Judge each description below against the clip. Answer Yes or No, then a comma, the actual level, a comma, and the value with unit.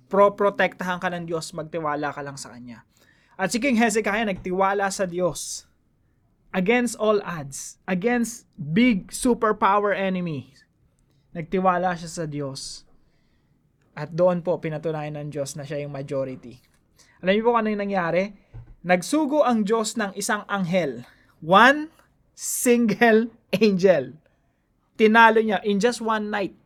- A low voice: No, medium, 185 Hz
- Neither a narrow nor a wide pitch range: No, wide, 6.5 semitones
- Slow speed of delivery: Yes, slow, 130 wpm